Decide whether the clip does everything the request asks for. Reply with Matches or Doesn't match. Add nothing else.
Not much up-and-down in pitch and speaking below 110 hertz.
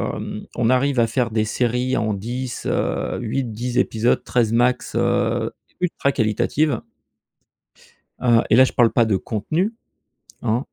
Doesn't match